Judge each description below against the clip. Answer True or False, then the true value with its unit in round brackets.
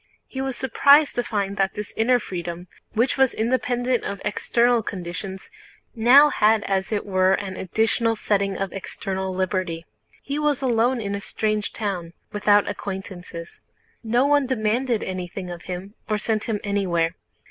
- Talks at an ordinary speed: True (155 wpm)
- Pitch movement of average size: True (4.1 semitones)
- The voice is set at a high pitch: True (210 Hz)